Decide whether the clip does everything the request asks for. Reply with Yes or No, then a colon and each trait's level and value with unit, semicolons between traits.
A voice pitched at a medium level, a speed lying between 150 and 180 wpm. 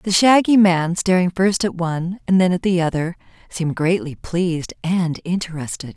Yes: medium, 175 Hz; average, 170 wpm